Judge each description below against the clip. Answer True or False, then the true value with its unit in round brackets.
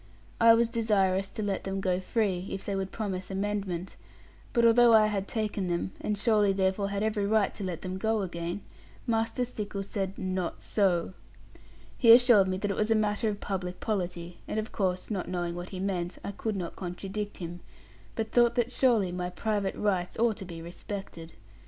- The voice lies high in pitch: True (195 Hz)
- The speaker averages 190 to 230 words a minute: True (195 wpm)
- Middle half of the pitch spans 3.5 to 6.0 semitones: False (2.8 semitones)